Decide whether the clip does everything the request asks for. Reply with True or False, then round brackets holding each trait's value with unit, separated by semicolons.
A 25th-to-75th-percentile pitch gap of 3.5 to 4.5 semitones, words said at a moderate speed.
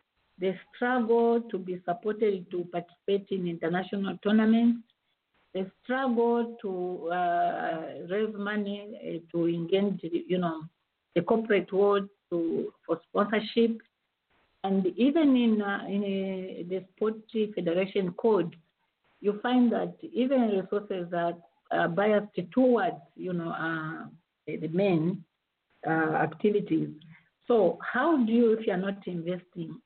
False (4.0 semitones; 125 wpm)